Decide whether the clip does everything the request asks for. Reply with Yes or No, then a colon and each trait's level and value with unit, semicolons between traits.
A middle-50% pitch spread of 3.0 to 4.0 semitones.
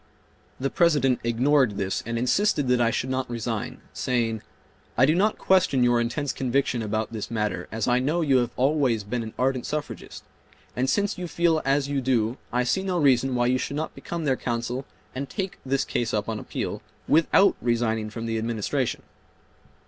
Yes: average, 3.6 semitones